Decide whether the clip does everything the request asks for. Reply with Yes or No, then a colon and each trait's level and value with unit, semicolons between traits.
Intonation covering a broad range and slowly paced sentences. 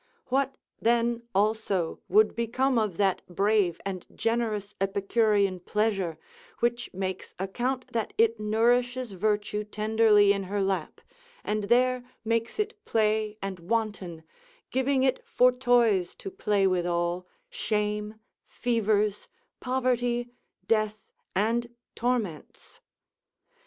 No: average, 3.3 semitones; slow, 110 wpm